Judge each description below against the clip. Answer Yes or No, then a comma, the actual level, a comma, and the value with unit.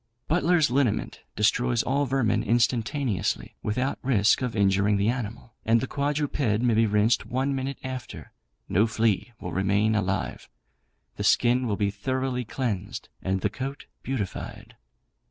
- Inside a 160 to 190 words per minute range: No, average, 140 wpm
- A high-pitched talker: No, low, 120 Hz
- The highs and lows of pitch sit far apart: No, average, 4.0 semitones